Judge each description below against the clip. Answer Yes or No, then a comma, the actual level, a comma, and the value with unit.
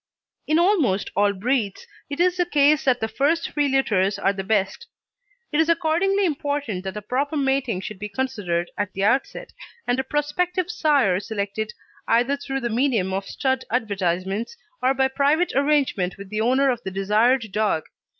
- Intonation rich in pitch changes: Yes, wide, 6.3 semitones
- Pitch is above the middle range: Yes, very high, 255 Hz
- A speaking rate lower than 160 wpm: No, average, 175 wpm